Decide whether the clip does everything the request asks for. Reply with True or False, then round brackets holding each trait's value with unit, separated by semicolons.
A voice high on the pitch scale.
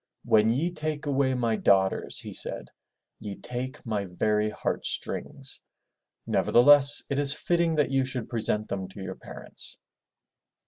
False (125 Hz)